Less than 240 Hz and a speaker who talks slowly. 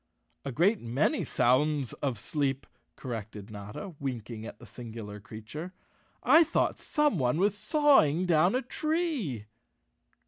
Yes: medium, 140 Hz; slow, 125 wpm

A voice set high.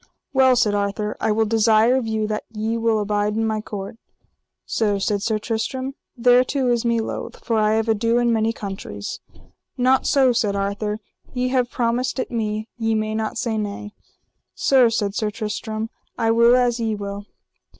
Yes: high, 220 Hz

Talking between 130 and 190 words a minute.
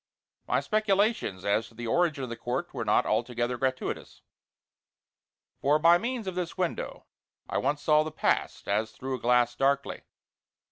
Yes: average, 160 wpm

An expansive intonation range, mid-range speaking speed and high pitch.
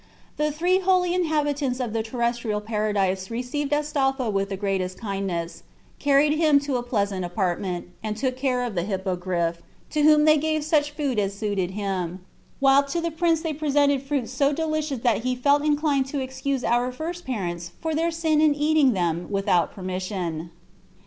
Yes: wide, 7.1 semitones; average, 175 wpm; very high, 255 Hz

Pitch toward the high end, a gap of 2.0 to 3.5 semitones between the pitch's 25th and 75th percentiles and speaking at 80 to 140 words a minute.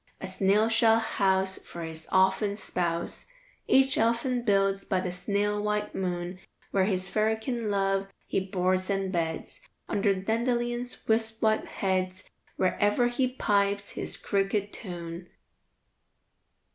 Yes: high, 200 Hz; average, 2.9 semitones; slow, 135 wpm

